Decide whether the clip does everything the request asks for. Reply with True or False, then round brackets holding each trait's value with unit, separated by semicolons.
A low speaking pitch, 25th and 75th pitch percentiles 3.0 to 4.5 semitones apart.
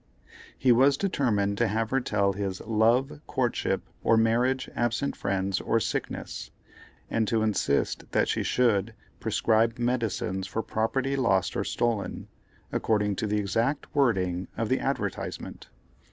True (115 Hz; 3.5 semitones)